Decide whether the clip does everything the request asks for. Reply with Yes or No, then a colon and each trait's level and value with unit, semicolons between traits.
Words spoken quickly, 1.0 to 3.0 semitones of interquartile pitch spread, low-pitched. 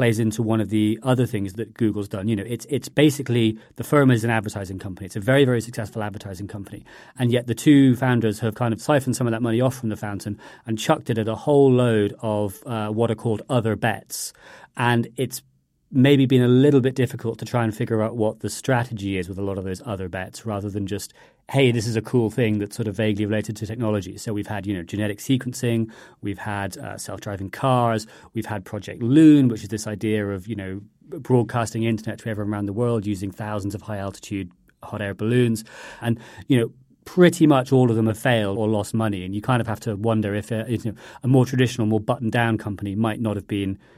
Yes: fast, 235 wpm; average, 2.7 semitones; low, 110 Hz